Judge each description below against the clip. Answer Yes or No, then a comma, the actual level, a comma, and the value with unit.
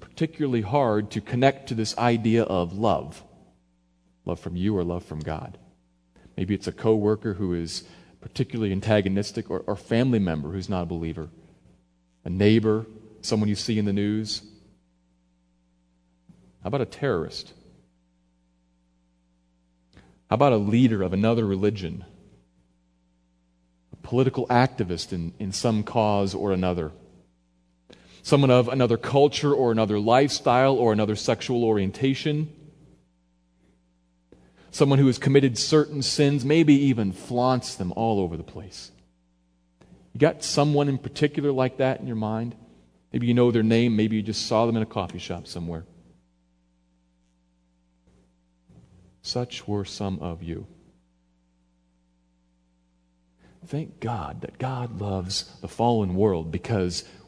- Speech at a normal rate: No, slow, 130 wpm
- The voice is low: Yes, very low, 95 Hz